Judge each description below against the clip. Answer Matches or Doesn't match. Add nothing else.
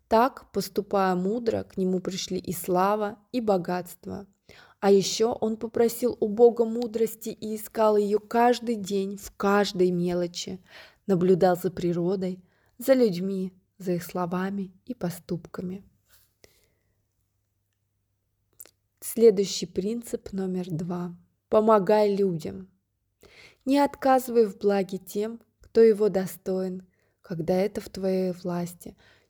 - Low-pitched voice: Doesn't match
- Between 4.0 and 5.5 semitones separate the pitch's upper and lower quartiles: Doesn't match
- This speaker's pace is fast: Doesn't match